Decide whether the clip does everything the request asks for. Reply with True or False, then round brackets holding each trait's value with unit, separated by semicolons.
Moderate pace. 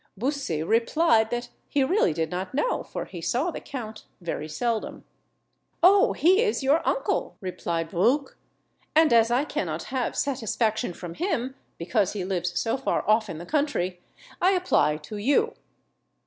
True (160 wpm)